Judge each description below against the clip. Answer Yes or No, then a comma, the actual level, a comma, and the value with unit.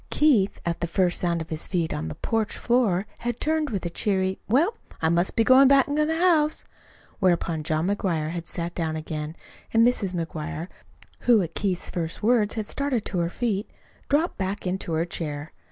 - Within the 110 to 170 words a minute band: No, average, 195 wpm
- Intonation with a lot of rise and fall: Yes, wide, 6.2 semitones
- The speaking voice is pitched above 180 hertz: Yes, high, 190 Hz